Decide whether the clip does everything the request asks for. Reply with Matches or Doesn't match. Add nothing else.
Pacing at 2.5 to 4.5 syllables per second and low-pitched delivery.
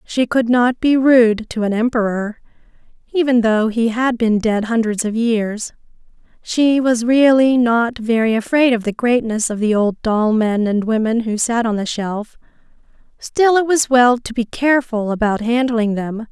Doesn't match